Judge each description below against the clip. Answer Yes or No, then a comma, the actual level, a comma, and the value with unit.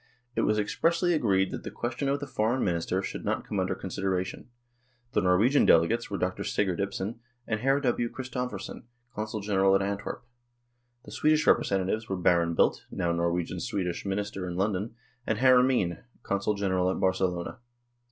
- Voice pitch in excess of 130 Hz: No, low, 100 Hz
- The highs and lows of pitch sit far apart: No, average, 4.1 semitones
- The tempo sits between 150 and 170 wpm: Yes, average, 165 wpm